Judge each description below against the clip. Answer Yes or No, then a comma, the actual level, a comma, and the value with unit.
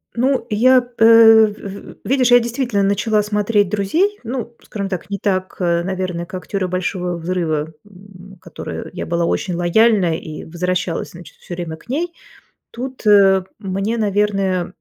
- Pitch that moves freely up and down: No, average, 3.7 semitones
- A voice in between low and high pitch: No, high, 195 Hz